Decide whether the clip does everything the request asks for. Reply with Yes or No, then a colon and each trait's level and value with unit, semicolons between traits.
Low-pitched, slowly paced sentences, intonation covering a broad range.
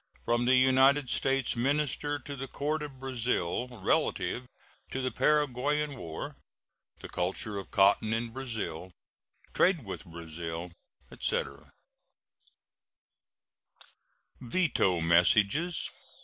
Yes: low, 125 Hz; slow, 100 wpm; wide, 6.4 semitones